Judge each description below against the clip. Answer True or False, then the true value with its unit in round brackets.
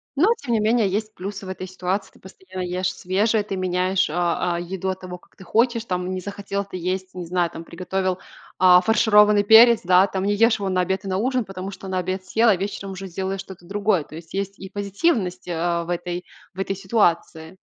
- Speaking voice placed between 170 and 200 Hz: True (190 Hz)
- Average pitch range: False (1.9 semitones)